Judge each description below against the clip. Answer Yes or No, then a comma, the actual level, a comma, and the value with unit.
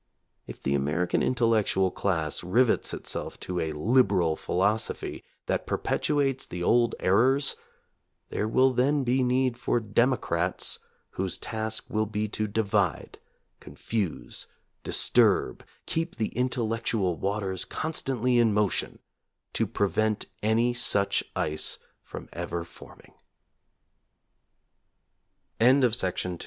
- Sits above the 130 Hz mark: No, low, 110 Hz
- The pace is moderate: No, slow, 110 wpm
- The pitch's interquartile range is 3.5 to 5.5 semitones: Yes, average, 4.7 semitones